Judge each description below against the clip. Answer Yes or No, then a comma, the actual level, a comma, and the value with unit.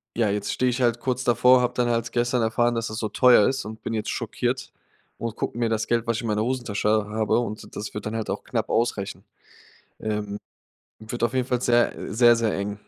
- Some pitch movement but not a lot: No, narrow, 2.0 semitones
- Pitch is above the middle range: No, low, 115 Hz